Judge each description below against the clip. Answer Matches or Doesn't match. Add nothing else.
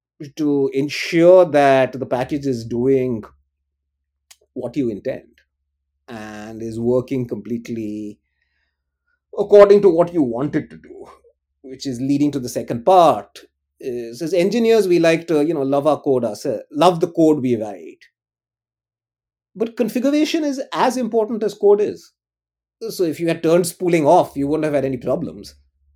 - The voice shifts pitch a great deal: Matches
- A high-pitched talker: Doesn't match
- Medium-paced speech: Matches